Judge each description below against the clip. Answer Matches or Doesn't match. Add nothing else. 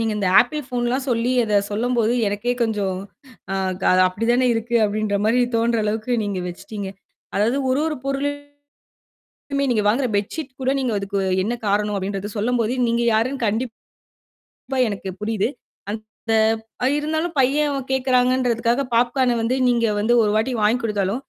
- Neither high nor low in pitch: Doesn't match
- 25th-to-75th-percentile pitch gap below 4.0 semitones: Matches